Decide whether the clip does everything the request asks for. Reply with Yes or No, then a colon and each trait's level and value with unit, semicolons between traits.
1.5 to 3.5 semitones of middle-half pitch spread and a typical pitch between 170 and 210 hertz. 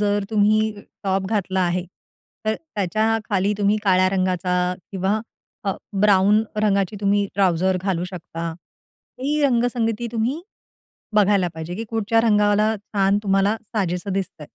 Yes: narrow, 2.4 semitones; high, 205 Hz